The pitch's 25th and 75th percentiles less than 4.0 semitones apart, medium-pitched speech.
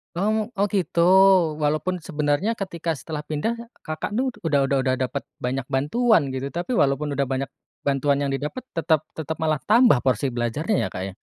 No: average, 4.7 semitones; medium, 150 Hz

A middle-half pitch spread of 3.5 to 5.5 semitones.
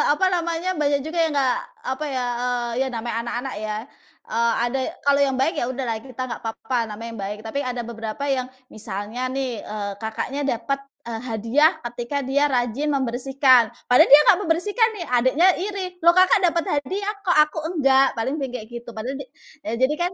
Yes: average, 4.1 semitones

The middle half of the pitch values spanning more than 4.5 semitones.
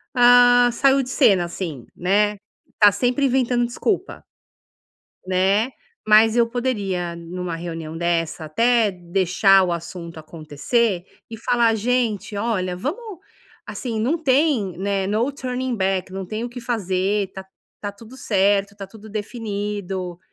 Yes: average, 4.9 semitones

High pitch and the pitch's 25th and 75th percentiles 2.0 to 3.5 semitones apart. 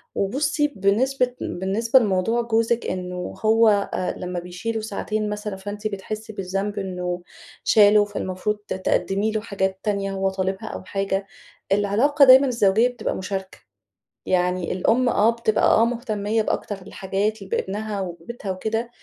Yes: high, 205 Hz; average, 2.9 semitones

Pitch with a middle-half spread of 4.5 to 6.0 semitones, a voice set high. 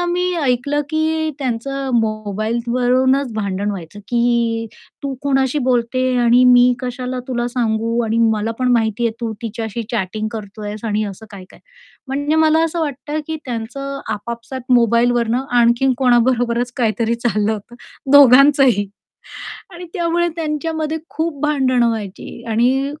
No: average, 3.4 semitones; high, 245 Hz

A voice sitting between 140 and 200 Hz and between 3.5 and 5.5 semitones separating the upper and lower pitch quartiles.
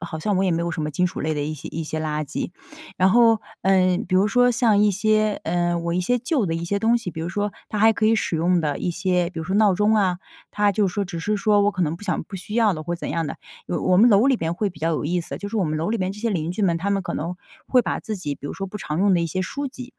Yes: medium, 185 Hz; average, 3.8 semitones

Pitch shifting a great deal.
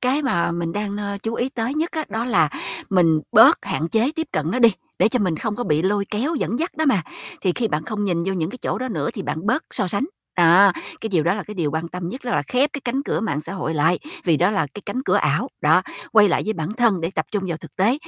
Yes: wide, 6.1 semitones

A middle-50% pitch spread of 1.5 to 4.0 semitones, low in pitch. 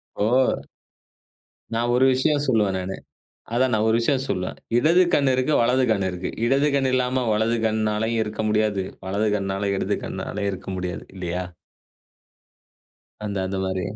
No: average, 4.7 semitones; low, 110 Hz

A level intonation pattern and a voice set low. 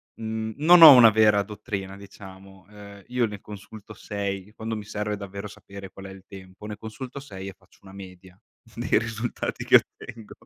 Yes: narrow, 2.2 semitones; low, 105 Hz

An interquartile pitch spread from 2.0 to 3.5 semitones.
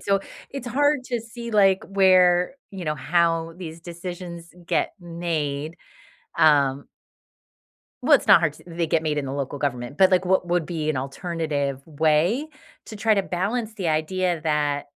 No: average, 3.9 semitones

